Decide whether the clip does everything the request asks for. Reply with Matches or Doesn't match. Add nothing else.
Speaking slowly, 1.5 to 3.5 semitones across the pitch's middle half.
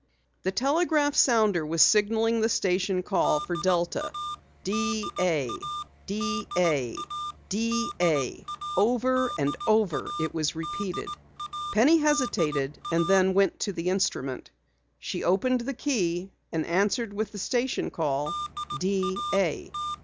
Doesn't match